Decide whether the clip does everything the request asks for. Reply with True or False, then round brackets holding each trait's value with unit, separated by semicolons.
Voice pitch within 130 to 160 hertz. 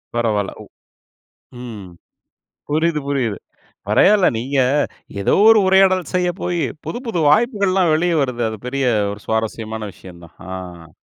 True (140 Hz)